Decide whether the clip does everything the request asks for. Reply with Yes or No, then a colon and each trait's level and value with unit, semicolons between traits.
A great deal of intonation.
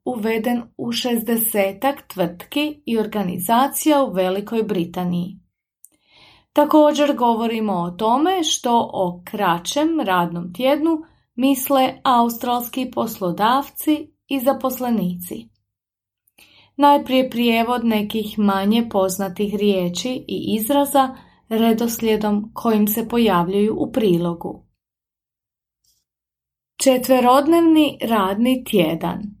Yes: wide, 5.8 semitones